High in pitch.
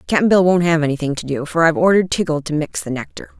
No: medium, 160 Hz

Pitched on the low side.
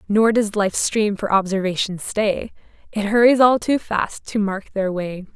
No: high, 205 Hz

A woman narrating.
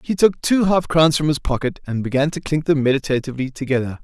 No: male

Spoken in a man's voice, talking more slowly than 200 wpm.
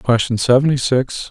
Yes: male; average, 140 wpm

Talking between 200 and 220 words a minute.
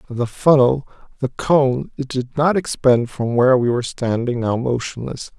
No: average, 155 wpm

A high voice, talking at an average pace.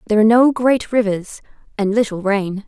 Yes: high, 215 Hz; average, 180 wpm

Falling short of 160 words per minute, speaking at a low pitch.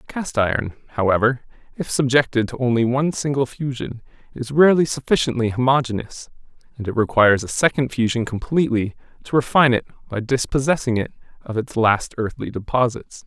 Yes: average, 145 wpm; low, 125 Hz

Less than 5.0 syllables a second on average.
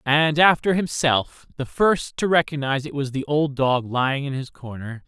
Yes: 4.7 syllables/s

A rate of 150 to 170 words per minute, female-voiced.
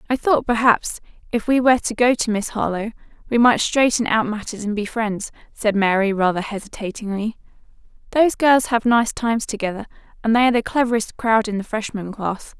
No: average, 185 wpm; female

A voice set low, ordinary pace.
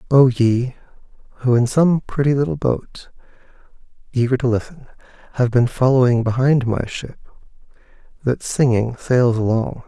No: low, 125 Hz; slow, 130 wpm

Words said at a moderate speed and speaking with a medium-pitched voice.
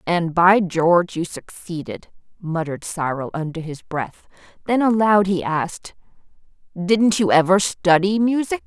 No: slow, 130 wpm; medium, 180 Hz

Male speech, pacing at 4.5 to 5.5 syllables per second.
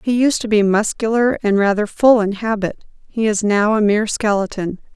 No: female; 5.1 syllables/s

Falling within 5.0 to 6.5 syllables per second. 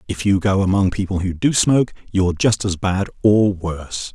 Yes: 5.2 syllables/s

